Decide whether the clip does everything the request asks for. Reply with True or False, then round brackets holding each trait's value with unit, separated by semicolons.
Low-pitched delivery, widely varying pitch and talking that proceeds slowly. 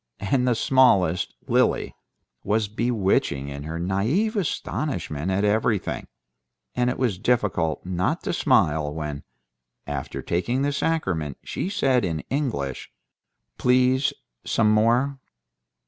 True (105 Hz; 7.2 semitones; 115 wpm)